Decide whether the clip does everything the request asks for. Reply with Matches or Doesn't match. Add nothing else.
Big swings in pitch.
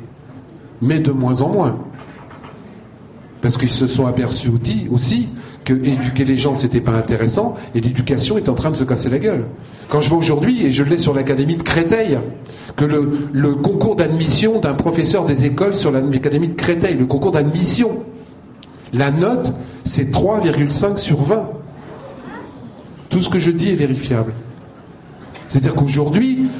Doesn't match